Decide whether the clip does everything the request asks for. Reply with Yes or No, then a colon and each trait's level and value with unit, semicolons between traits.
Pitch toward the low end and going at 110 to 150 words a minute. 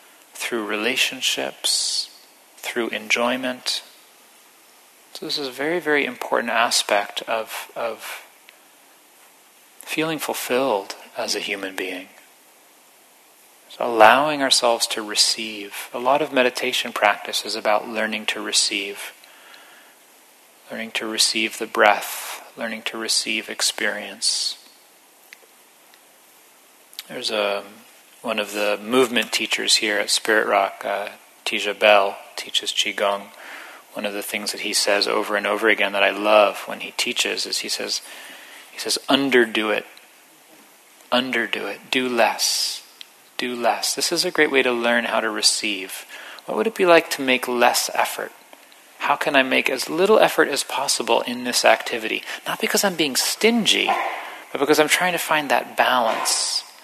Yes: low, 120 Hz; average, 145 wpm